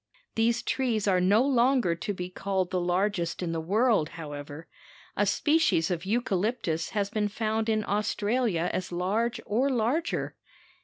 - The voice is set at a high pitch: Yes, high, 205 Hz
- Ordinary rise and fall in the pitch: Yes, average, 4.6 semitones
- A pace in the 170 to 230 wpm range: No, average, 150 wpm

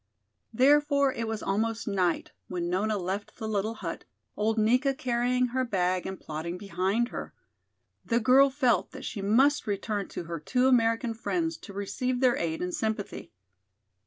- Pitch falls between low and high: No, high, 220 Hz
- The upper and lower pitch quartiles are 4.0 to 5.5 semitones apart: Yes, average, 4.6 semitones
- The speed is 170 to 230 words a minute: No, average, 160 wpm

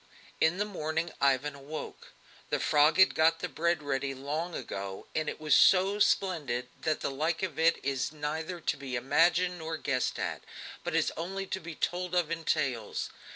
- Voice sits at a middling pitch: Yes, medium, 160 Hz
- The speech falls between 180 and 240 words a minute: Yes, average, 185 wpm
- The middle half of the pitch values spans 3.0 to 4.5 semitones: Yes, average, 3.7 semitones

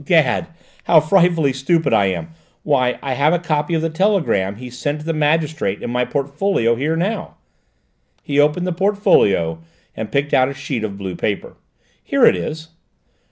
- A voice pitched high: No, medium, 145 Hz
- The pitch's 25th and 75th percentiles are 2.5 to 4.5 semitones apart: No, average, 5.0 semitones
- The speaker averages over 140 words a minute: Yes, average, 170 wpm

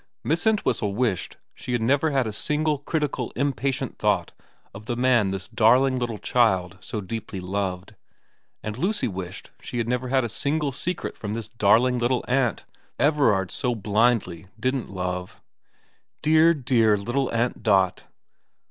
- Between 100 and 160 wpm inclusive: Yes, average, 150 wpm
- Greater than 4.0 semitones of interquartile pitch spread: Yes, average, 4.7 semitones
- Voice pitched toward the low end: Yes, low, 120 Hz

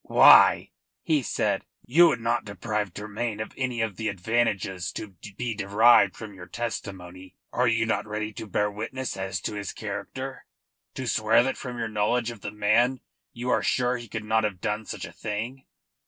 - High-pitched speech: No, low, 110 Hz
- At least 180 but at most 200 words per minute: Yes, average, 185 wpm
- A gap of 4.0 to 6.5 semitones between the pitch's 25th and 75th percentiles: No, average, 2.7 semitones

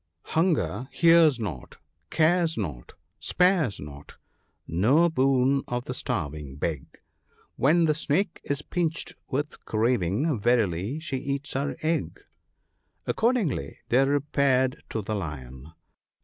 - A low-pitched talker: Yes, low, 130 Hz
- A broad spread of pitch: Yes, wide, 8.4 semitones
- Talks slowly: Yes, slow, 120 wpm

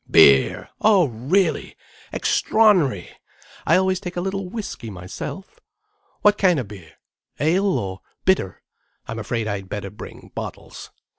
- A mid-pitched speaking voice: Yes, medium, 160 Hz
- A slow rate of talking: Yes, slow, 125 wpm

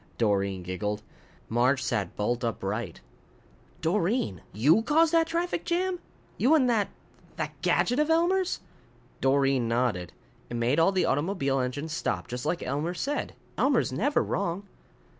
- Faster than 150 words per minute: No, average, 140 wpm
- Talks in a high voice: No, medium, 145 Hz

